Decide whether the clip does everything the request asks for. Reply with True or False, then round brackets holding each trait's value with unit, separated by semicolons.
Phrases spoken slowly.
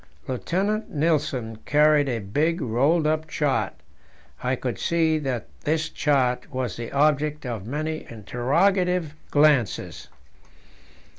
True (115 wpm)